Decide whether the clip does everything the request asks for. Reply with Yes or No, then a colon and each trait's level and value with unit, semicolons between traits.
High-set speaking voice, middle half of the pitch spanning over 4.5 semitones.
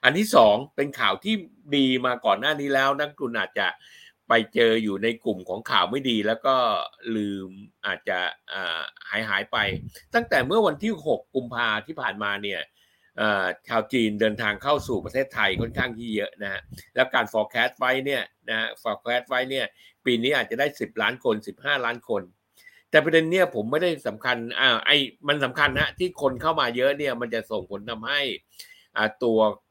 No: low, 125 Hz; average, 5.0 semitones